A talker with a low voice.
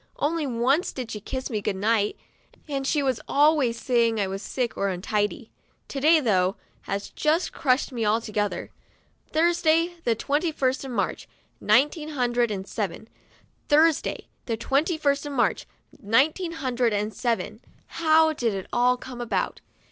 No: very high, 250 Hz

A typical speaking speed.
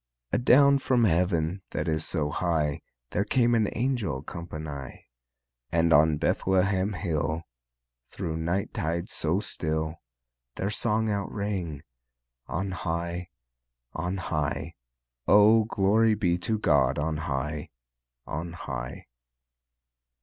No: slow, 115 wpm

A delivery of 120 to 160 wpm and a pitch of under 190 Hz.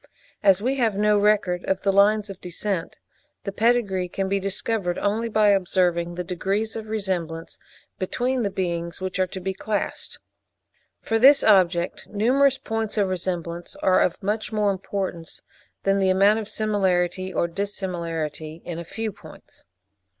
No: average, 155 wpm; high, 195 Hz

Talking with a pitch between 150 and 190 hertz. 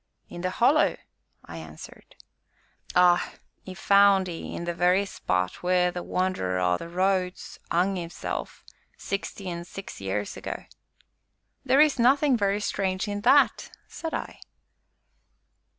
Yes: medium, 185 Hz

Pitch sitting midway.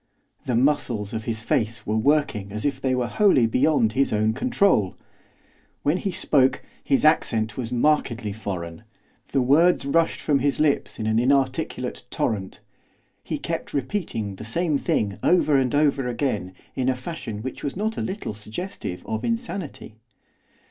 No: low, 130 Hz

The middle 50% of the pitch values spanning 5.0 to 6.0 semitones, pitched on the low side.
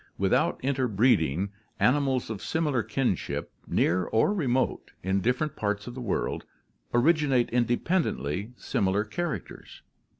Yes: average, 5.3 semitones; low, 120 Hz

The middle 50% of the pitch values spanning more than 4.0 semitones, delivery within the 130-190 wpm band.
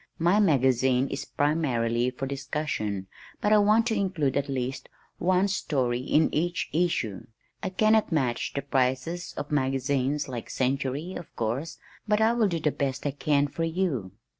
Yes: average, 5.1 semitones; average, 165 wpm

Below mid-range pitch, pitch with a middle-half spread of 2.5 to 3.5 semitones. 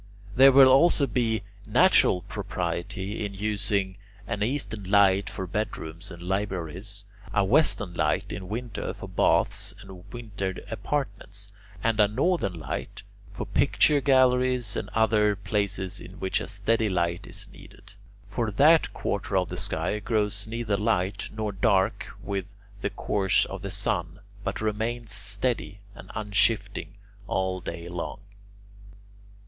Yes: low, 100 Hz; average, 2.9 semitones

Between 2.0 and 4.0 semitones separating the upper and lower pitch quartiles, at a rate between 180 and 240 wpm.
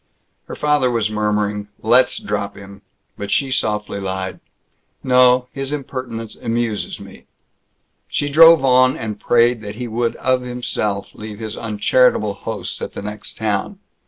No: average, 3.4 semitones; average, 145 wpm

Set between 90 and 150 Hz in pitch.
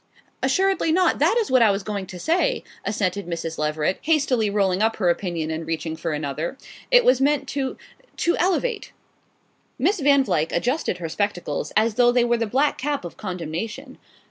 No: high, 215 Hz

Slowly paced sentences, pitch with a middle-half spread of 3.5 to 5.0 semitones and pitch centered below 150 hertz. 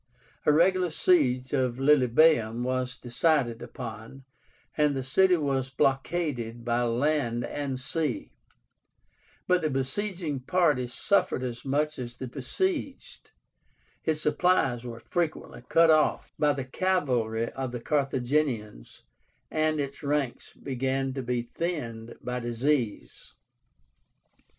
Yes: slow, 115 wpm; average, 4.0 semitones; low, 135 Hz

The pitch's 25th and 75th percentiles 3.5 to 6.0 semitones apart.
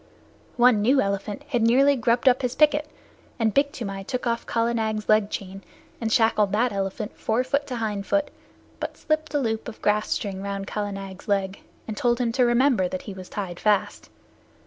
Yes: average, 3.8 semitones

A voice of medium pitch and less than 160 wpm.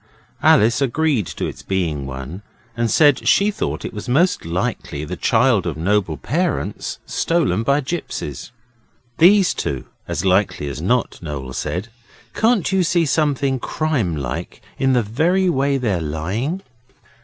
No: low, 120 Hz; average, 145 wpm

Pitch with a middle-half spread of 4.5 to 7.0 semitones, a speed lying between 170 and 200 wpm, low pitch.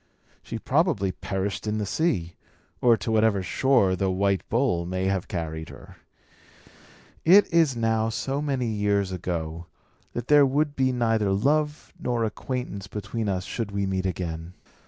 No: average, 5.2 semitones; average, 155 wpm; low, 105 Hz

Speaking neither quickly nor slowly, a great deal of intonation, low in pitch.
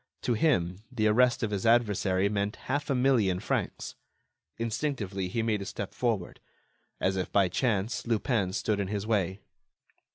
No: average, 160 wpm; average, 3.6 semitones; low, 105 Hz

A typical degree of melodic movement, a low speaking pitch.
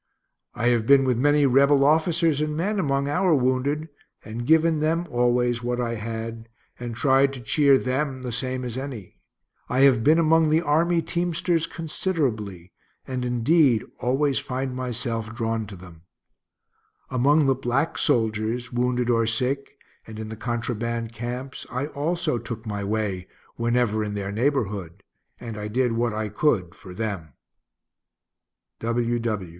Yes: average, 4.2 semitones; low, 125 Hz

